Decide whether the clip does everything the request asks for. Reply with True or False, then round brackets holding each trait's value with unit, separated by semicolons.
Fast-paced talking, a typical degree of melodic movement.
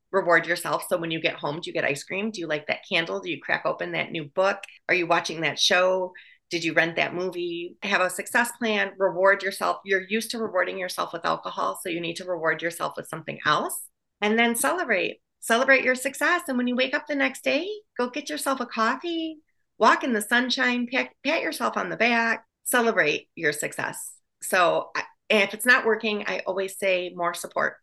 False (210 wpm; 6.1 semitones)